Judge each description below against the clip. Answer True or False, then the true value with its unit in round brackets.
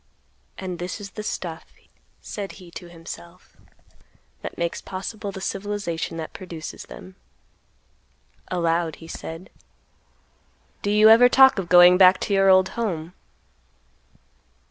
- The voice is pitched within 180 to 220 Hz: True (185 Hz)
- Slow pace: True (125 wpm)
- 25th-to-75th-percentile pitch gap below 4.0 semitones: True (2.8 semitones)